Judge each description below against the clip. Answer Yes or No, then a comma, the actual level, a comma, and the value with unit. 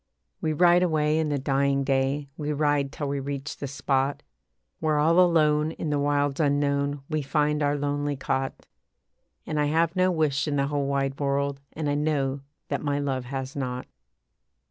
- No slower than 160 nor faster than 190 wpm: Yes, average, 180 wpm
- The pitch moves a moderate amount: No, narrow, 1.5 semitones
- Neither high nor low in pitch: Yes, medium, 145 Hz